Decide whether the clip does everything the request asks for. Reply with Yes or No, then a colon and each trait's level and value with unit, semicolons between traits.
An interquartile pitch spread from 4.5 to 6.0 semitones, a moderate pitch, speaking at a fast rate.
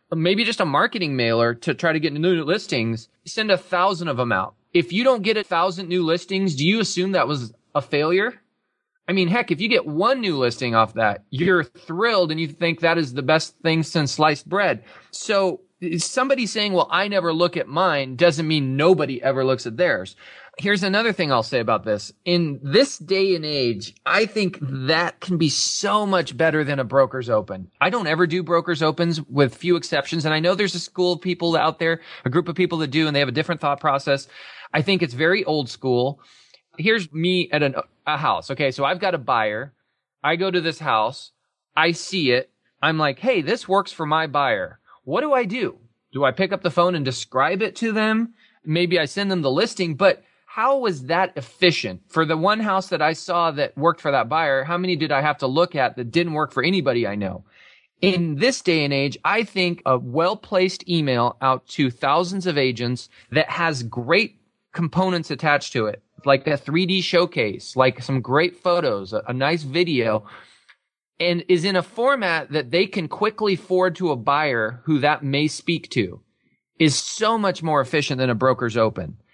Yes: average, 4.9 semitones; medium, 165 Hz; fast, 210 wpm